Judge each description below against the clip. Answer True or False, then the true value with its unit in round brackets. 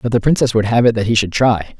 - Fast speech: True (335 wpm)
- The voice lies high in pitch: False (115 Hz)